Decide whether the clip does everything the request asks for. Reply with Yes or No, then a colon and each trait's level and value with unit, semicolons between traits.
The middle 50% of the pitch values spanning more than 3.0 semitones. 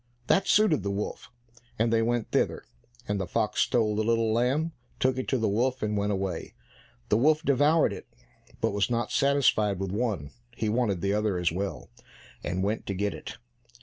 Yes: average, 3.9 semitones